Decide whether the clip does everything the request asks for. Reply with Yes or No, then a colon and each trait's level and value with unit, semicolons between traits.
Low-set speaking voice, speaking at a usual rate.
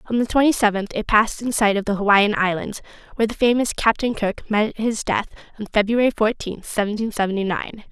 No: high, 215 Hz; average, 195 wpm